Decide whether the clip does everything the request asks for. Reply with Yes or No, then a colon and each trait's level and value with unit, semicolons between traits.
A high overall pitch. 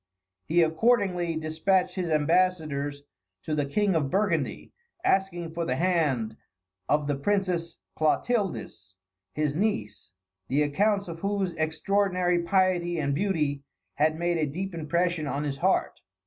No: medium, 170 Hz